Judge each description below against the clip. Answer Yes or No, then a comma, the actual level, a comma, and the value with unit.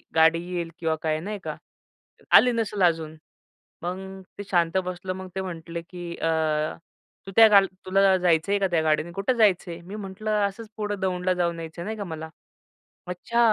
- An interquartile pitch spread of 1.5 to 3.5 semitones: Yes, average, 2.9 semitones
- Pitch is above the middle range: No, medium, 180 Hz